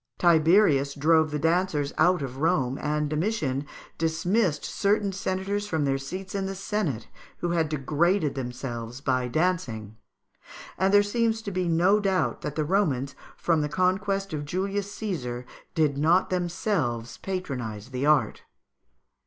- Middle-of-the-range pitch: Yes, medium, 160 Hz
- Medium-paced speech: Yes, average, 145 wpm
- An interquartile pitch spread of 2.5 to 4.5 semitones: No, wide, 5.5 semitones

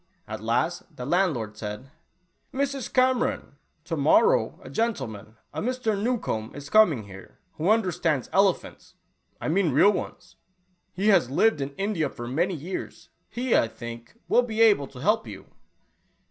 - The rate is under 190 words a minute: Yes, average, 160 wpm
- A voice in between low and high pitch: Yes, medium, 175 Hz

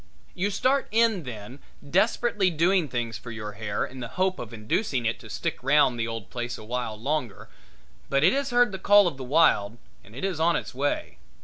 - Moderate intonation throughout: No, wide, 8.4 semitones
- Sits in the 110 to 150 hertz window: Yes, low, 135 Hz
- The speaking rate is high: Yes, fast, 210 wpm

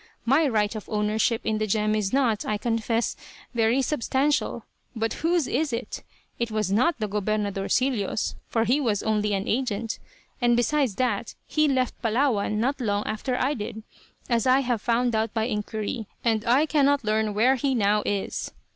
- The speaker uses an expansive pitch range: No, average, 3.3 semitones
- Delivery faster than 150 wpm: Yes, average, 175 wpm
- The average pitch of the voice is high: Yes, high, 230 Hz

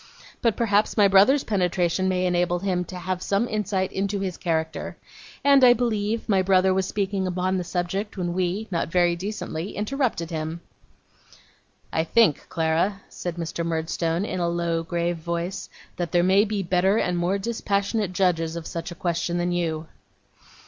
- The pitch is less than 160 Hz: No, medium, 185 Hz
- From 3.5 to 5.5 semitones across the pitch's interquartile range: No, average, 2.7 semitones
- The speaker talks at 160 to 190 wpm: Yes, average, 170 wpm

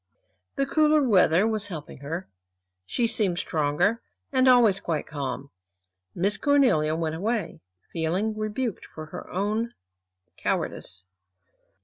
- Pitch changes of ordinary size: No, wide, 6.4 semitones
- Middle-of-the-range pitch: No, high, 195 Hz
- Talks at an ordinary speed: No, slow, 115 wpm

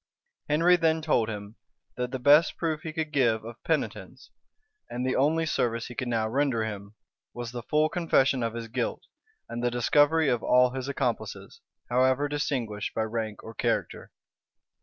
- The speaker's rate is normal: Yes, average, 170 wpm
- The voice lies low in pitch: Yes, low, 125 Hz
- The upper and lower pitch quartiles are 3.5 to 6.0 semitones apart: Yes, average, 4.4 semitones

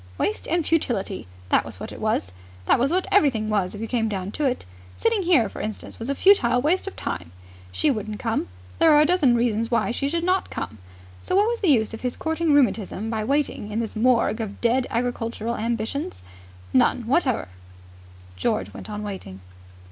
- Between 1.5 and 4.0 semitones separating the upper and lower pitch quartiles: No, wide, 5.6 semitones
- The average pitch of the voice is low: No, high, 235 Hz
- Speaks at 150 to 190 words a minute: No, average, 200 wpm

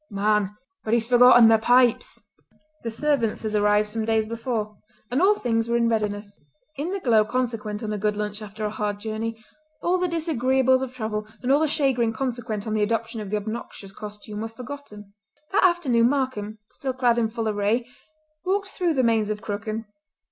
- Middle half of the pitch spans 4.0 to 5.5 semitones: No, average, 3.3 semitones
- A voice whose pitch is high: Yes, high, 225 Hz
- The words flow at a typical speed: Yes, average, 190 wpm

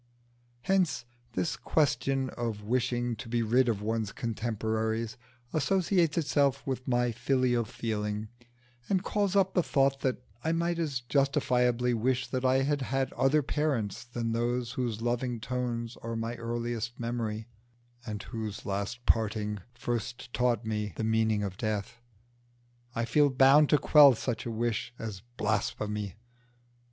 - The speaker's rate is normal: Yes, average, 145 wpm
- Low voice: Yes, low, 120 Hz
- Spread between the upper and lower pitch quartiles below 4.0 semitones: Yes, average, 3.1 semitones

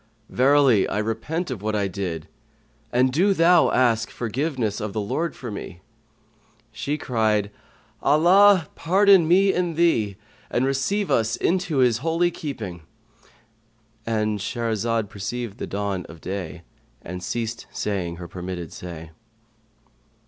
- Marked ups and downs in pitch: Yes, wide, 6.7 semitones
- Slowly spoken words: Yes, slow, 125 wpm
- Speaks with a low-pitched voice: Yes, low, 115 Hz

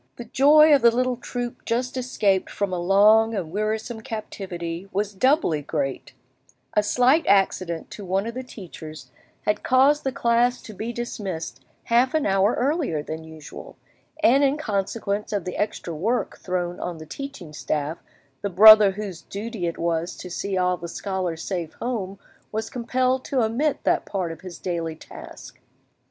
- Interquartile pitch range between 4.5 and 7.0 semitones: Yes, wide, 5.5 semitones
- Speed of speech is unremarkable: Yes, average, 170 wpm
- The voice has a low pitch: No, high, 205 Hz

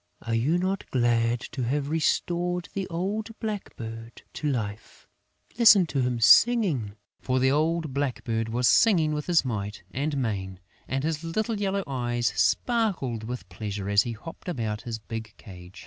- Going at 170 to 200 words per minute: No, average, 155 wpm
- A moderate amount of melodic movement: No, wide, 7.1 semitones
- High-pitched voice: No, low, 130 Hz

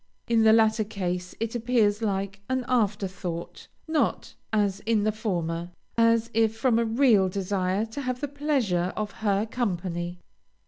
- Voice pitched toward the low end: No, high, 215 Hz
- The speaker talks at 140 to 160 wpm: Yes, average, 155 wpm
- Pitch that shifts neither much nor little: Yes, average, 3.3 semitones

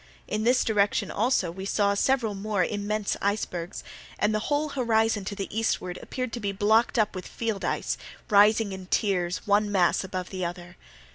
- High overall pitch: Yes, high, 205 Hz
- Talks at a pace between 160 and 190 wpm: Yes, average, 180 wpm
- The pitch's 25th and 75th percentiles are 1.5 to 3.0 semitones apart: Yes, narrow, 2.6 semitones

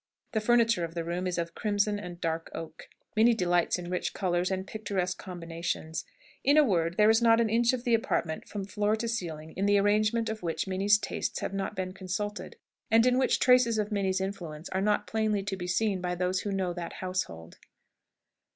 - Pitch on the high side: Yes, high, 195 Hz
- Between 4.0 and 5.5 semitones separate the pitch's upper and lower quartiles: No, average, 3.5 semitones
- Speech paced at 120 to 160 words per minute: No, fast, 205 wpm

